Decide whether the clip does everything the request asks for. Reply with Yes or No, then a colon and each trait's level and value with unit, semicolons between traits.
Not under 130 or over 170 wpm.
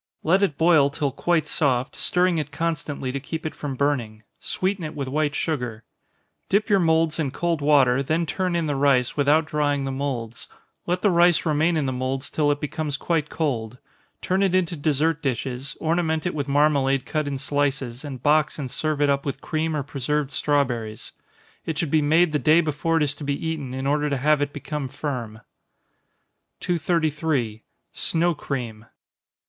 No: average, 185 wpm